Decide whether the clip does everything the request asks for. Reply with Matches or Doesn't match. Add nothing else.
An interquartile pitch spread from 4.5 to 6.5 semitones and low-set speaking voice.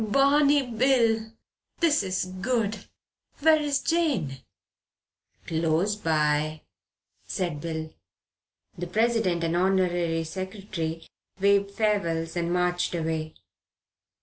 Doesn't match